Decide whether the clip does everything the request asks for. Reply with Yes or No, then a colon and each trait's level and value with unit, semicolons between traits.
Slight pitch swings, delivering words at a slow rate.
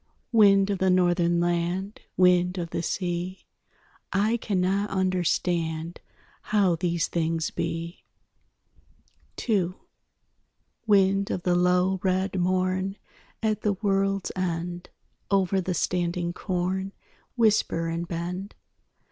Yes: narrow, 2.0 semitones; slow, 105 wpm